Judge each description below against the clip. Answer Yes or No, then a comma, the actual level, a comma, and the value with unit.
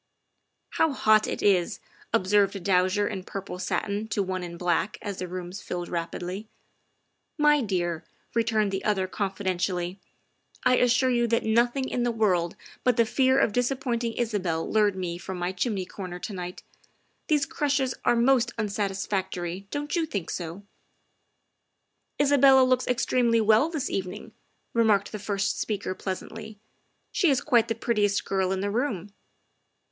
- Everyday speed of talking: Yes, average, 170 wpm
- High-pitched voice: Yes, high, 205 Hz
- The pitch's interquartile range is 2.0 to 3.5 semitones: No, average, 4.4 semitones